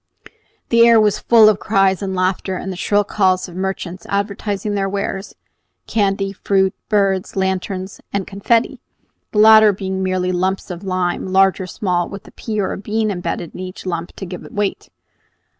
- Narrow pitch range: Yes, narrow, 1.7 semitones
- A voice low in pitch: No, high, 195 Hz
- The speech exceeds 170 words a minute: Yes, average, 180 wpm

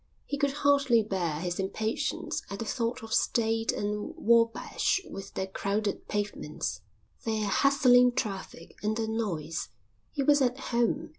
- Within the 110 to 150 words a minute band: Yes, average, 145 wpm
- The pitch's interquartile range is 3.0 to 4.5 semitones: Yes, average, 3.7 semitones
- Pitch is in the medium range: No, high, 220 Hz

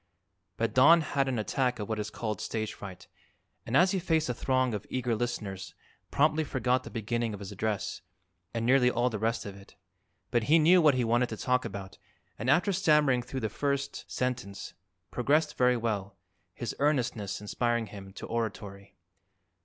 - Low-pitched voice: Yes, low, 120 Hz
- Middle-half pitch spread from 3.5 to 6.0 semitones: Yes, average, 4.1 semitones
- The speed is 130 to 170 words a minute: No, average, 180 wpm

